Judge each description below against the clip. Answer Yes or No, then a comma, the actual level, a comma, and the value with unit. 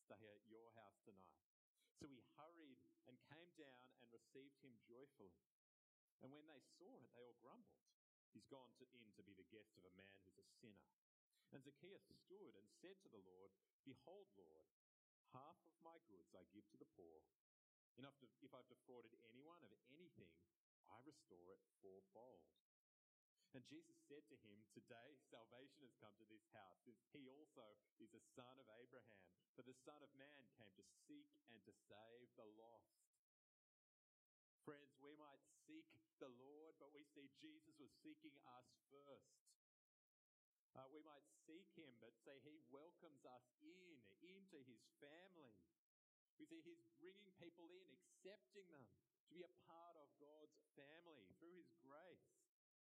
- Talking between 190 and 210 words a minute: No, average, 165 wpm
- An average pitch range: No, wide, 7.0 semitones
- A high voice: No, low, 135 Hz